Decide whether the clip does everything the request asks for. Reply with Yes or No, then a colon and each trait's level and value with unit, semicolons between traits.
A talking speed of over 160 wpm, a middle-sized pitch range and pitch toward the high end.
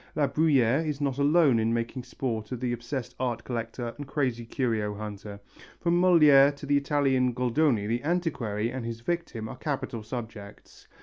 No: average, 170 wpm; average, 3.9 semitones; low, 125 Hz